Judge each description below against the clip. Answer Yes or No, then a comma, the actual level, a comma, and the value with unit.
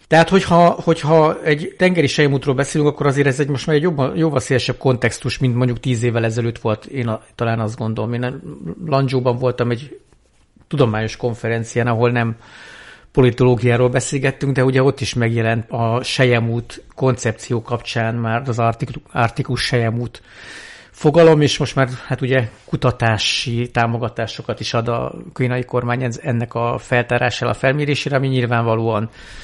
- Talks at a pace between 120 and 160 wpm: Yes, average, 145 wpm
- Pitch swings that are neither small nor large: Yes, average, 3.1 semitones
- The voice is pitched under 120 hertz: No, low, 125 Hz